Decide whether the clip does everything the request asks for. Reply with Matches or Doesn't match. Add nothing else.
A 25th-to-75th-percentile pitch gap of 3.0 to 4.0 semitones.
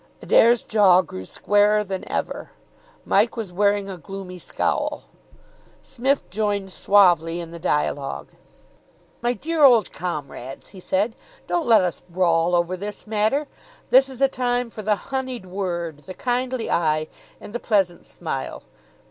Doesn't match